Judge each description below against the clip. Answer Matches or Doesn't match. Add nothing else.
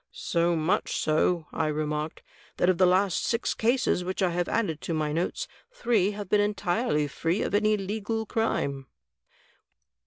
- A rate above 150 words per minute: Matches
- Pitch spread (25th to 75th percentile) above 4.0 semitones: Matches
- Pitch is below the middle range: Doesn't match